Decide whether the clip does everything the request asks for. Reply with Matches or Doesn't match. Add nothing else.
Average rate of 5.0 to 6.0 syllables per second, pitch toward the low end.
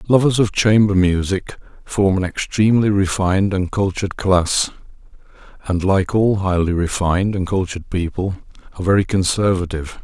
Matches